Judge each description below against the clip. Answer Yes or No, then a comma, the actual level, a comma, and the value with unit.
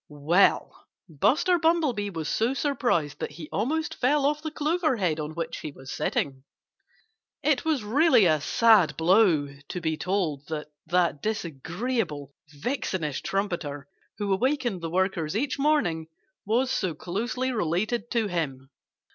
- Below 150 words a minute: Yes, average, 140 wpm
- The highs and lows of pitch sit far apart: Yes, wide, 8.3 semitones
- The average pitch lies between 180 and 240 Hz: Yes, high, 190 Hz